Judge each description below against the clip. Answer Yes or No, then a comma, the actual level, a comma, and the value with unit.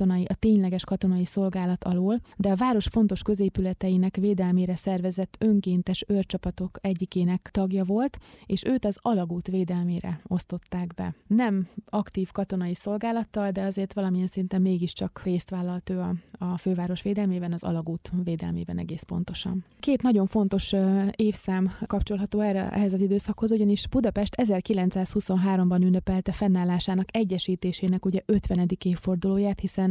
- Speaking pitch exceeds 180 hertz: Yes, high, 190 Hz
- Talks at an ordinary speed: Yes, average, 130 wpm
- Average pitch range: No, narrow, 2.0 semitones